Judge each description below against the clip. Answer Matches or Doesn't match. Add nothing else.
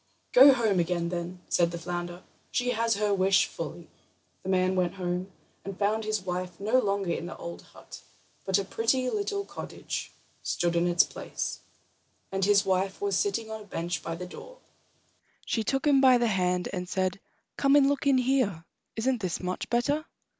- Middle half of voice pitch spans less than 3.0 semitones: Doesn't match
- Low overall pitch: Doesn't match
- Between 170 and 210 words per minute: Matches